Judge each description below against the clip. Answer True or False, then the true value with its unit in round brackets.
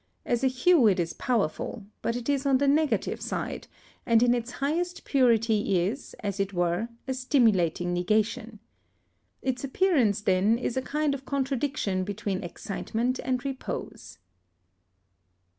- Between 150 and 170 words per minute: False (140 wpm)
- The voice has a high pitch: True (240 Hz)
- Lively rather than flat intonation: False (4.9 semitones)